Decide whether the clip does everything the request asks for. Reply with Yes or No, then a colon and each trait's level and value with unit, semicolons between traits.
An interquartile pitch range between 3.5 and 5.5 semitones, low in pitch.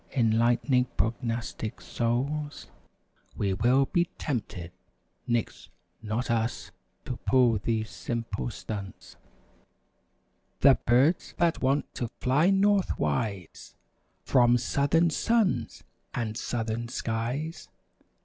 Yes: average, 3.8 semitones; low, 120 Hz